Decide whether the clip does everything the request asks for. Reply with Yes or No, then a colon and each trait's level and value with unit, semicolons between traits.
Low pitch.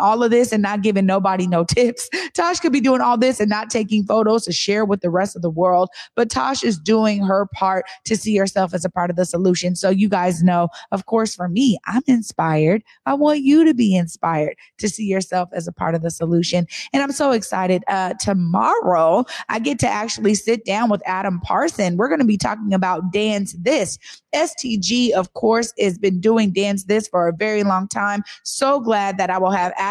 No: high, 200 Hz